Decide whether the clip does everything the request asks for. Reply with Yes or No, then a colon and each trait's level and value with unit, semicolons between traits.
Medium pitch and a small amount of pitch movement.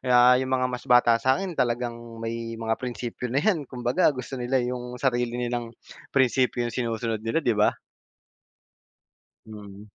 No: low, 120 Hz; narrow, 1.7 semitones